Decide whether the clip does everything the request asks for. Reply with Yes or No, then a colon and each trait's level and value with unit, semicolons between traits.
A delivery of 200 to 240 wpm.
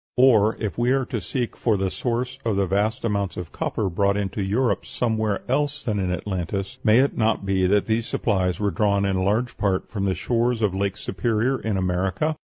Yes: fast, 205 wpm